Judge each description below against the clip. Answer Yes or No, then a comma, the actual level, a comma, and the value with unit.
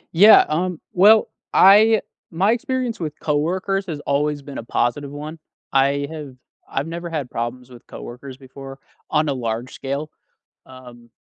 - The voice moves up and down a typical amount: Yes, average, 4.9 semitones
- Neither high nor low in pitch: Yes, medium, 145 Hz